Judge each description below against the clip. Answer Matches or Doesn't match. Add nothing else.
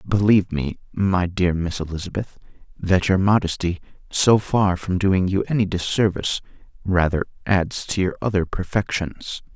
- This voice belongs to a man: Matches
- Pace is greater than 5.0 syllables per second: Doesn't match